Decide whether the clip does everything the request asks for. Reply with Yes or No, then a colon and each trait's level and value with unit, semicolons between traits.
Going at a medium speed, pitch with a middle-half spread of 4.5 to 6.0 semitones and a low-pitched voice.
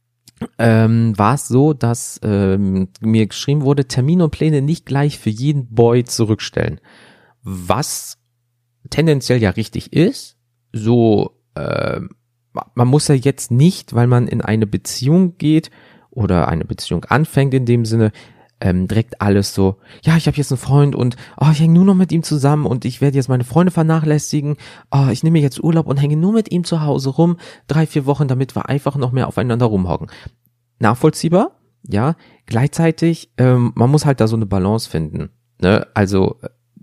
Yes: average, 175 wpm; average, 4.8 semitones; low, 125 Hz